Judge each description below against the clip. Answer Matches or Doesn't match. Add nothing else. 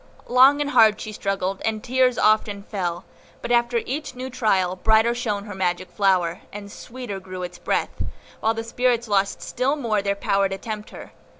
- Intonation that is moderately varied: Matches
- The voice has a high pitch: Matches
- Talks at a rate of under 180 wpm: Doesn't match